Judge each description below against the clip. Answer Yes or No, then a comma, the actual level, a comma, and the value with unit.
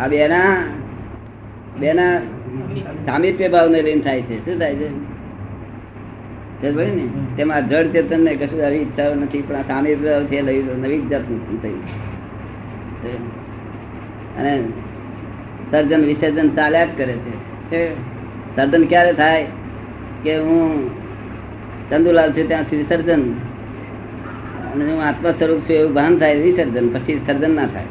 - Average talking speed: Yes, average, 110 wpm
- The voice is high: No, low, 135 Hz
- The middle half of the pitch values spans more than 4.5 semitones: Yes, average, 4.9 semitones